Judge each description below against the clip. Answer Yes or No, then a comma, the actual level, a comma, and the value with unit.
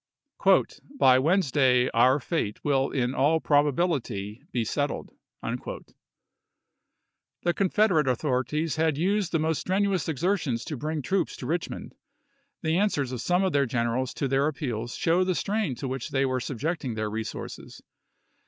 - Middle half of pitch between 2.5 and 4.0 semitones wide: No, average, 4.8 semitones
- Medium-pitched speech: Yes, medium, 145 Hz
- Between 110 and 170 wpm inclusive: Yes, average, 150 wpm